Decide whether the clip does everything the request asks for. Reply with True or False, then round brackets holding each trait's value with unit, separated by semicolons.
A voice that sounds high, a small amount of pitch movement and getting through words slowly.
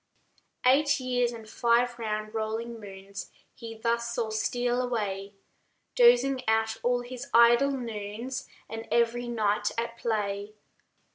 True (235 Hz; 2.1 semitones; 130 wpm)